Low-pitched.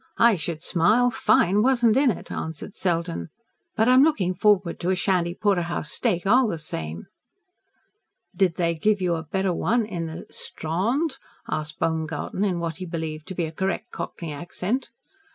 No: medium, 180 Hz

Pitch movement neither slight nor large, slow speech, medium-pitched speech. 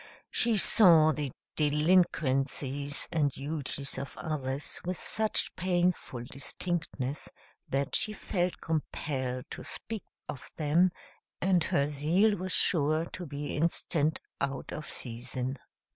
Yes: average, 4.1 semitones; slow, 115 wpm; medium, 150 Hz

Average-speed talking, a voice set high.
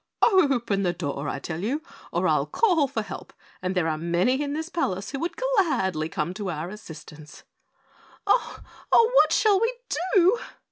Yes: average, 175 wpm; high, 210 Hz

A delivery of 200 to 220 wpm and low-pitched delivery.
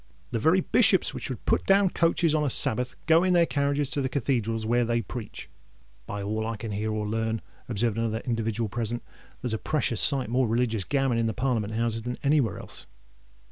Yes: fast, 205 wpm; low, 120 Hz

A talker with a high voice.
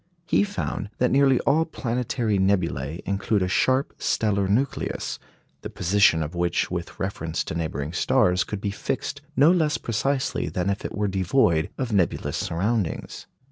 No: low, 100 Hz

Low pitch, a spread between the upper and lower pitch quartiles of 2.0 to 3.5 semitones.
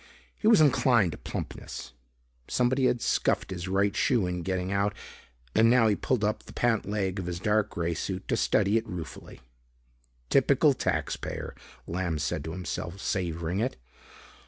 No: low, 100 Hz; average, 4.2 semitones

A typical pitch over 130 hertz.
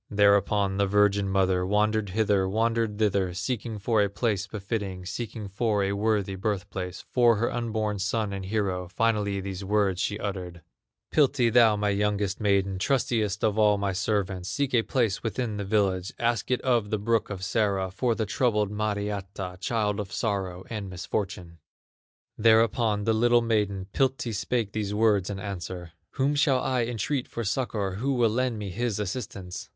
No: low, 105 Hz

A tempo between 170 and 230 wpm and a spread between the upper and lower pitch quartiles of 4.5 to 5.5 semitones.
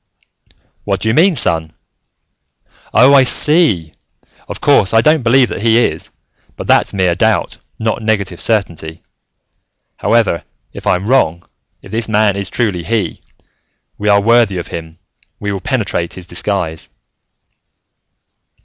No: average, 140 wpm; average, 4.9 semitones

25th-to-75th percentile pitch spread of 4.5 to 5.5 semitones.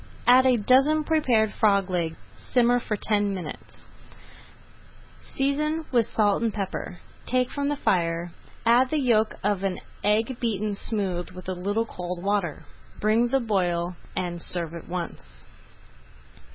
Yes: average, 5.2 semitones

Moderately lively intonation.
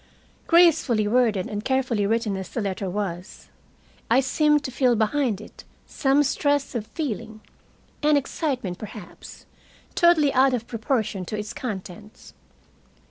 Yes: average, 4.8 semitones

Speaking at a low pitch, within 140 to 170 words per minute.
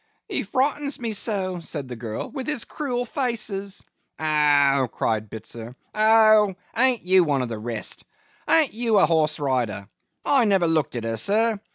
No: medium, 185 Hz; average, 165 wpm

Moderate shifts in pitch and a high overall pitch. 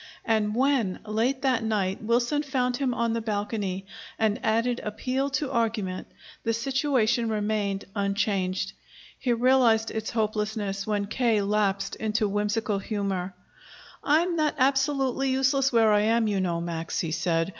Yes: average, 3.7 semitones; high, 220 Hz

